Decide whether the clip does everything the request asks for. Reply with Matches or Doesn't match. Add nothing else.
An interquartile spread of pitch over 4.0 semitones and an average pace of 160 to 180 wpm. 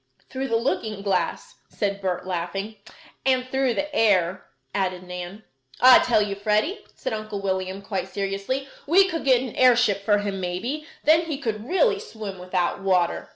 Matches